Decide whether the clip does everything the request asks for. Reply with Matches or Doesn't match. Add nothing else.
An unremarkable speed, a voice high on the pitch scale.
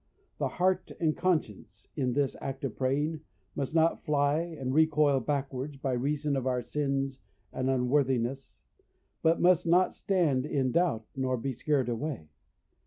Doesn't match